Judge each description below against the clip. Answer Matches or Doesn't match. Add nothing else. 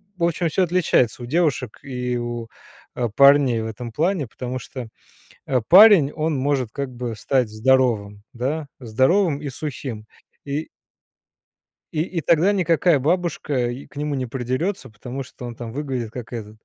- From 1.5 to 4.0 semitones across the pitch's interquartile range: Doesn't match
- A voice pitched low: Matches